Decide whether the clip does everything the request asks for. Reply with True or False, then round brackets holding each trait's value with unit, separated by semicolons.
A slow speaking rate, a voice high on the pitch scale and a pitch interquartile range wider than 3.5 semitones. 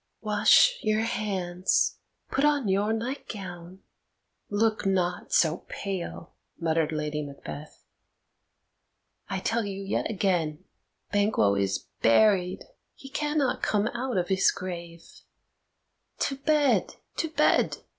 True (110 wpm; 195 Hz; 4.7 semitones)